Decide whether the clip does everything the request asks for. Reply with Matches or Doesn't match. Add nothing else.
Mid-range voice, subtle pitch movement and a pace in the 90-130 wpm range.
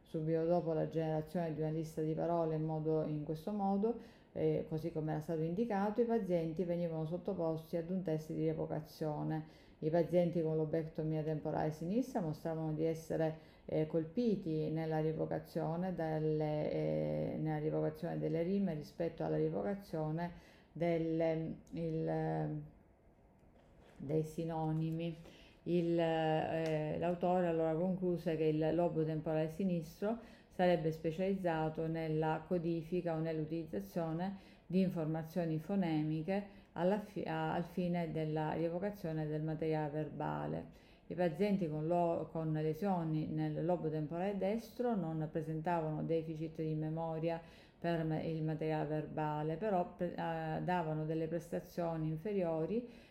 Matches